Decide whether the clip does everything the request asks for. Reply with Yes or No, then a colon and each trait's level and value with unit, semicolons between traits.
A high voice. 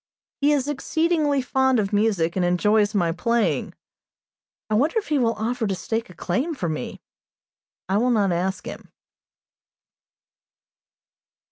Yes: high, 220 Hz